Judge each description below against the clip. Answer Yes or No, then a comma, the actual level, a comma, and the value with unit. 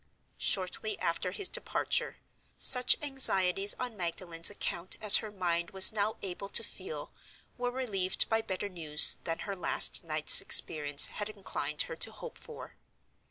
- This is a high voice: Yes, high, 195 Hz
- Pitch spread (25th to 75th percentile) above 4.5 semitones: No, average, 4.2 semitones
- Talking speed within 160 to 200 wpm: No, average, 150 wpm